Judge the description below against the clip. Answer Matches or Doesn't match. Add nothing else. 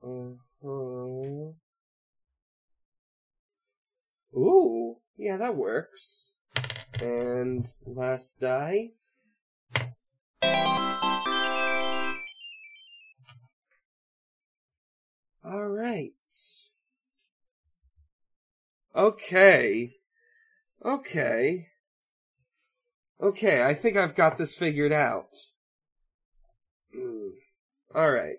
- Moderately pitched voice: Matches